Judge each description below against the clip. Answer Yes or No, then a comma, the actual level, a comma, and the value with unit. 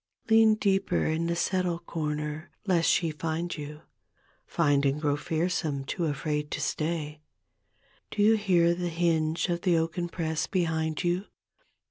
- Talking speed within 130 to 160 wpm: Yes, average, 145 wpm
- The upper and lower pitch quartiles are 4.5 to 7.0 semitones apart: No, narrow, 2.5 semitones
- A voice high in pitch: No, medium, 165 Hz